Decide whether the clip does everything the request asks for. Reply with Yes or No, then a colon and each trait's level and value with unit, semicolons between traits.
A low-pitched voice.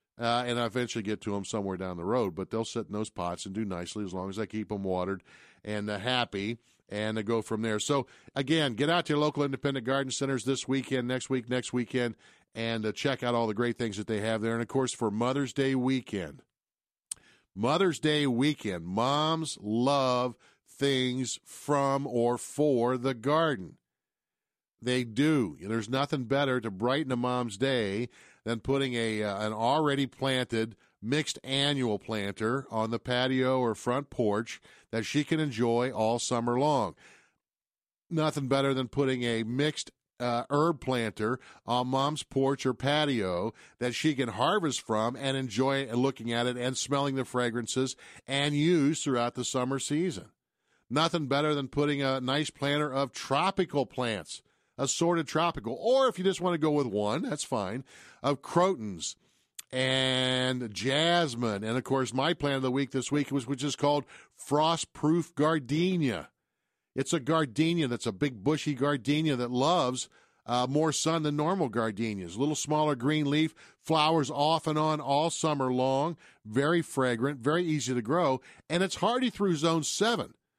Yes: low, 130 Hz